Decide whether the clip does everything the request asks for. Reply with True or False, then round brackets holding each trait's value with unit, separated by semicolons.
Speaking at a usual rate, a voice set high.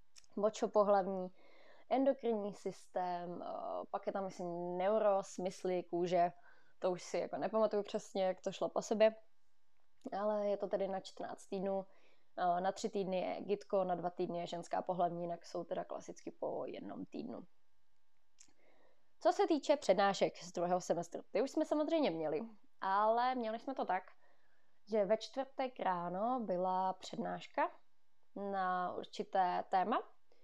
True (140 wpm; 195 Hz)